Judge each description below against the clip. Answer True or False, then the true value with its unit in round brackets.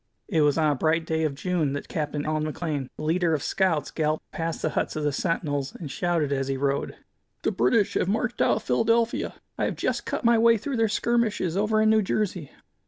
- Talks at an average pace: False (225 wpm)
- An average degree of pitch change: False (6.1 semitones)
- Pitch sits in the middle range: True (165 Hz)